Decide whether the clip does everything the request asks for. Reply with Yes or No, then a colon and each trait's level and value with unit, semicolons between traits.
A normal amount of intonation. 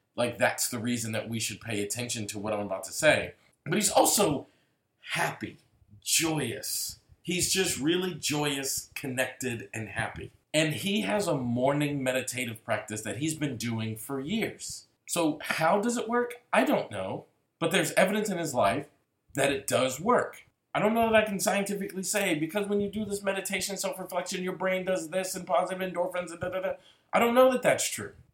No: wide, 8.1 semitones